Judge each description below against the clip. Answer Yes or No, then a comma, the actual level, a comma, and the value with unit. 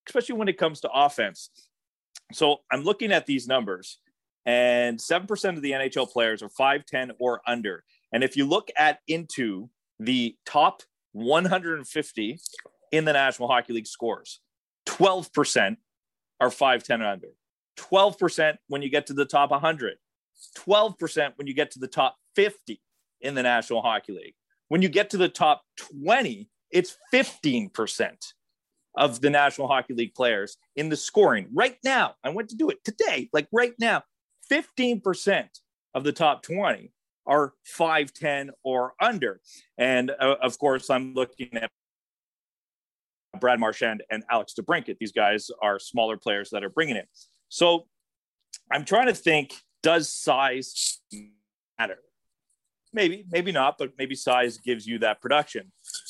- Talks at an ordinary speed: Yes, average, 155 wpm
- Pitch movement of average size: No, wide, 7.3 semitones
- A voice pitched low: No, medium, 150 Hz